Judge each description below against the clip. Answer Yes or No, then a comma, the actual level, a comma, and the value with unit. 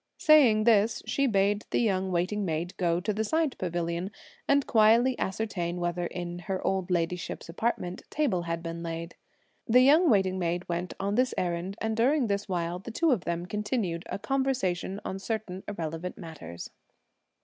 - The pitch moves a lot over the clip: No, average, 4.3 semitones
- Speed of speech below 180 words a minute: Yes, average, 170 wpm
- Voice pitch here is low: No, high, 190 Hz